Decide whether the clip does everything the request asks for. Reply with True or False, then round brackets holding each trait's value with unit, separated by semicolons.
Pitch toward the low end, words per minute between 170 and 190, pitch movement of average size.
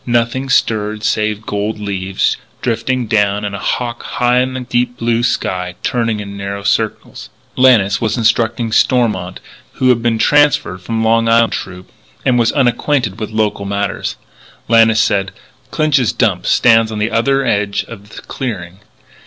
False (115 Hz; 160 wpm; 3.0 semitones)